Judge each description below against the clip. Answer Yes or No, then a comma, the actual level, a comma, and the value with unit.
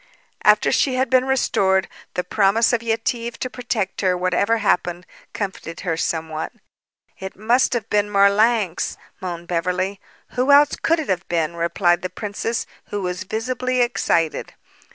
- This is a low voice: No, high, 200 Hz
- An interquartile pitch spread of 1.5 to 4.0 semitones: No, average, 4.7 semitones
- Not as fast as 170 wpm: Yes, average, 150 wpm